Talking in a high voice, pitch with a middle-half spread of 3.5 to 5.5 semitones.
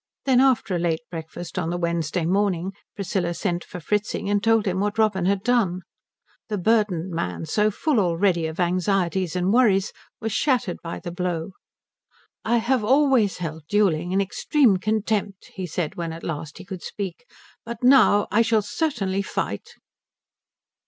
Yes: high, 195 Hz; average, 3.8 semitones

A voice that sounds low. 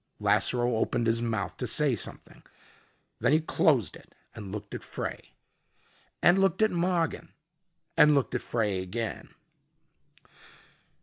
Yes: low, 120 Hz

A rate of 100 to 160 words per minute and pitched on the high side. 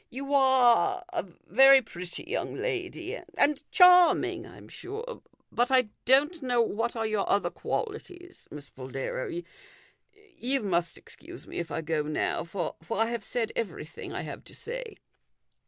Yes: average, 155 wpm; very high, 250 Hz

